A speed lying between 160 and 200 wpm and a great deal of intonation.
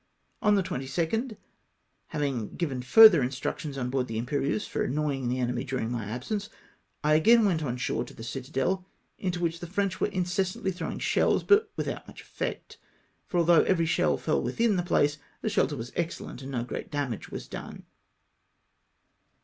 Yes: average, 180 wpm; wide, 6.4 semitones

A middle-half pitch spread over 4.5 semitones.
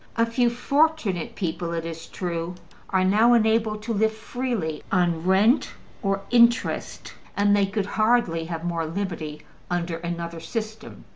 Yes: average, 5.1 semitones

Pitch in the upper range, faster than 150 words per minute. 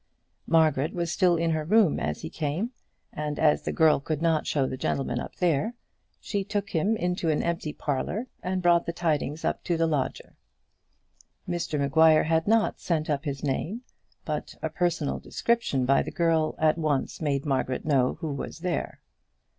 No: medium, 160 Hz; average, 180 wpm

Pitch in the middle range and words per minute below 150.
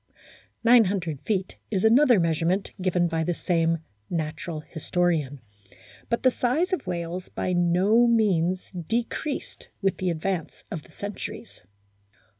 Yes: medium, 180 Hz; average, 140 wpm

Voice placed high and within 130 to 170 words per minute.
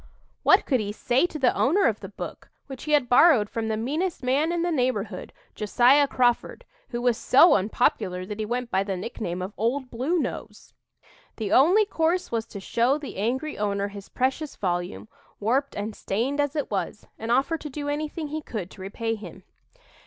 No: high, 245 Hz; average, 195 wpm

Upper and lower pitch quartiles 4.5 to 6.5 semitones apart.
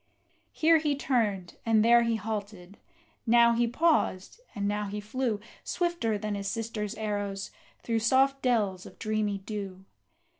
No: average, 2.7 semitones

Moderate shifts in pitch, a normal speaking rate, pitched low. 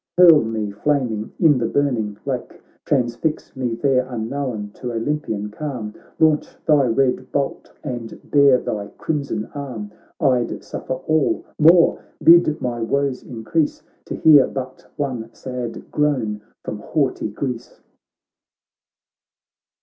No: average, 4.3 semitones; slow, 130 wpm; low, 130 Hz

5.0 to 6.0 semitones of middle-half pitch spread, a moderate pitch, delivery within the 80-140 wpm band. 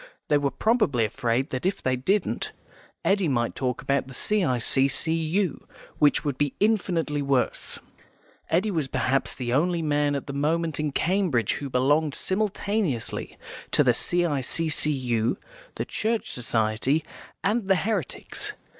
Yes: wide, 5.6 semitones; medium, 145 Hz; slow, 135 wpm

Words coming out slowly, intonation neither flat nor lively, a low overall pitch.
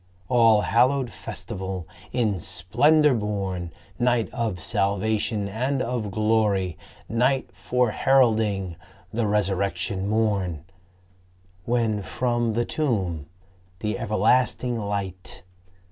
Yes: slow, 95 wpm; average, 3.6 semitones; low, 110 Hz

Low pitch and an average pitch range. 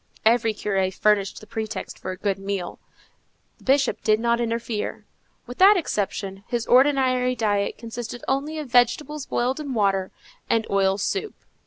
No: high, 230 Hz; average, 4.0 semitones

